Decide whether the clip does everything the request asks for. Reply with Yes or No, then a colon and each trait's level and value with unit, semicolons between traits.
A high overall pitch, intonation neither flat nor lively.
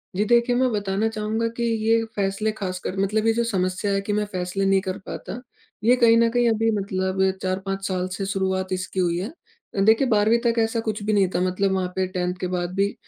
Yes: high, 200 Hz; average, 3.0 semitones